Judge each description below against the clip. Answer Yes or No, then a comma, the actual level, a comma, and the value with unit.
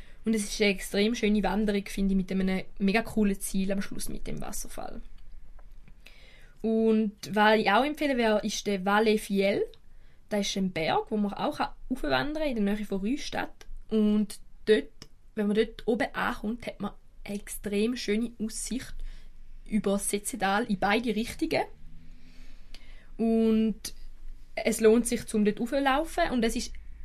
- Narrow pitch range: Yes, narrow, 2.2 semitones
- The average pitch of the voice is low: No, high, 215 Hz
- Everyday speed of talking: Yes, average, 160 wpm